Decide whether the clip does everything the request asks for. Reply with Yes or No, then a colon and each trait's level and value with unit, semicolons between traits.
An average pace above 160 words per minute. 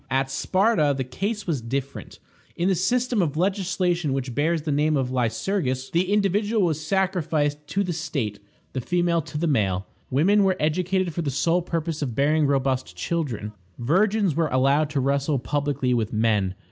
Yes: average, 170 wpm